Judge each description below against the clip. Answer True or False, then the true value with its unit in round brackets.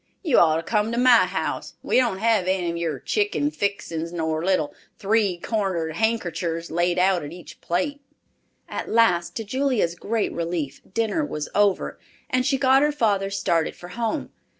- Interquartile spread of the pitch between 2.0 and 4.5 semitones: False (5.2 semitones)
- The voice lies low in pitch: False (190 Hz)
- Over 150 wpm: True (170 wpm)